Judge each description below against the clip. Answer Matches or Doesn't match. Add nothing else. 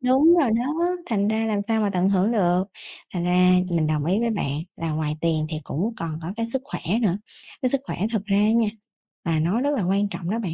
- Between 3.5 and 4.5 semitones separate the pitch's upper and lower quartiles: Doesn't match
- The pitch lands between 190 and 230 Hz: Matches